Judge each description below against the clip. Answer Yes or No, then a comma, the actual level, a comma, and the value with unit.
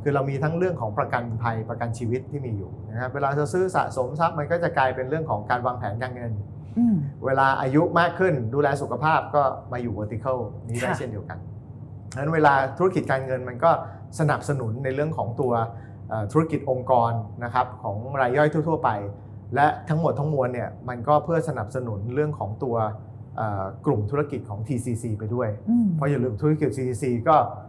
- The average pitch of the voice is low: Yes, low, 130 Hz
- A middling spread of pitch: Yes, average, 4.2 semitones